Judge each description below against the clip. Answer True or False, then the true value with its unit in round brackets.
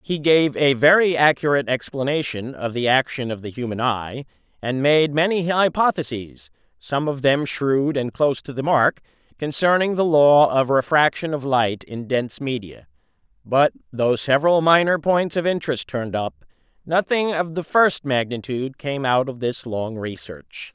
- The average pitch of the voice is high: False (140 Hz)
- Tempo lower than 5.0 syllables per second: True (4.7 syllables/s)